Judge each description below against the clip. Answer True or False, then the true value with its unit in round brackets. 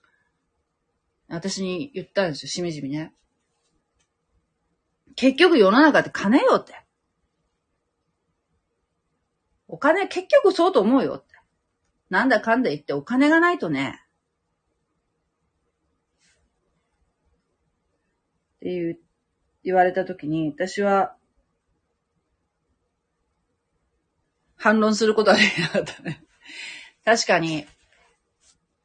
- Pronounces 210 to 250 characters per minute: False (170 characters per minute)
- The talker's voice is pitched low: False (160 Hz)